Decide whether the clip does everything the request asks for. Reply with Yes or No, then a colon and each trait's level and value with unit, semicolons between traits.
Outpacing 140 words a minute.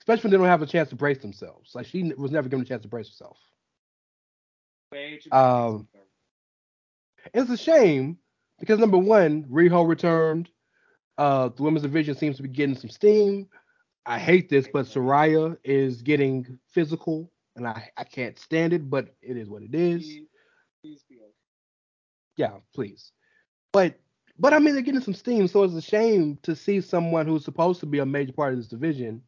Yes: average, 175 wpm